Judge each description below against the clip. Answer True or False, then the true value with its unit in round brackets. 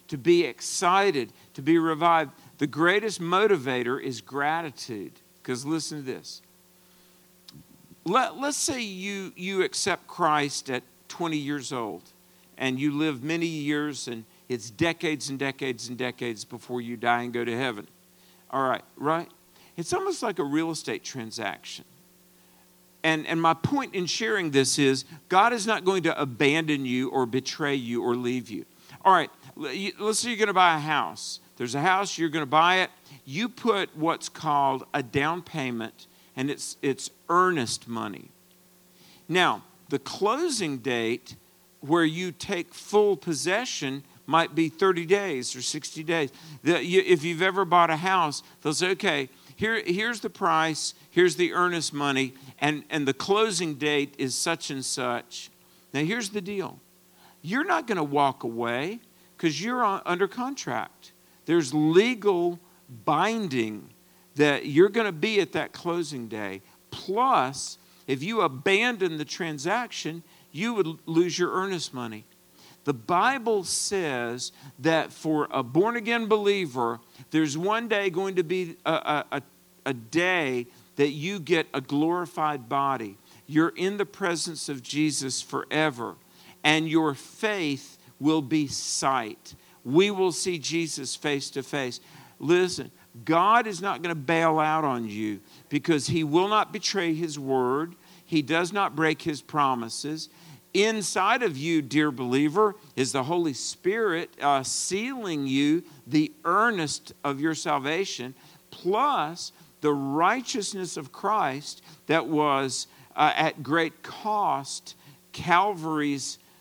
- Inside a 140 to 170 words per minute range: True (145 wpm)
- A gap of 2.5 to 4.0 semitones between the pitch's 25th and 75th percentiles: False (4.9 semitones)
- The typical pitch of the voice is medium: True (155 Hz)